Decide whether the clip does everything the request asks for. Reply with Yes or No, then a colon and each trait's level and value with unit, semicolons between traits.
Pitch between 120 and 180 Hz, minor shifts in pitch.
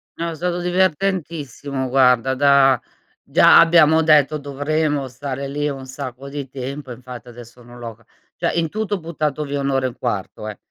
No: medium, 140 Hz; average, 3.2 semitones